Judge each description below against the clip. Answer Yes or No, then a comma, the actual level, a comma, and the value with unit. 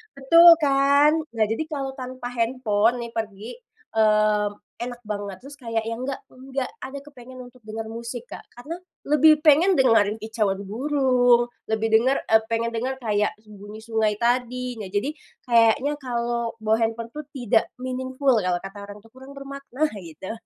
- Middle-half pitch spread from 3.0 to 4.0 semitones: Yes, average, 3.4 semitones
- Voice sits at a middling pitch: No, high, 240 Hz